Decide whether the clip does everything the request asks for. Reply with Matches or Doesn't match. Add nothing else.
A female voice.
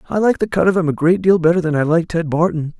Doesn't match